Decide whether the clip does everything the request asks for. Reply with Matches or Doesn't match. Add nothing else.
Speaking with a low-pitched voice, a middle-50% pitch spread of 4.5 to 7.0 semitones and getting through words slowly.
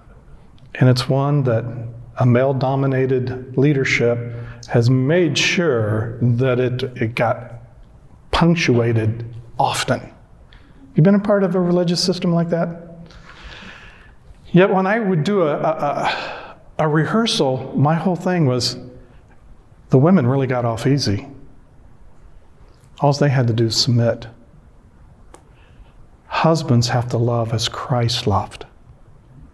Matches